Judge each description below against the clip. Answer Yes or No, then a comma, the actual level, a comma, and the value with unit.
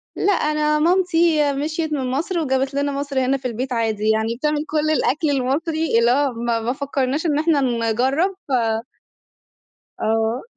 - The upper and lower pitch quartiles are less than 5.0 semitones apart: Yes, average, 3.6 semitones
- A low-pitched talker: No, very high, 280 Hz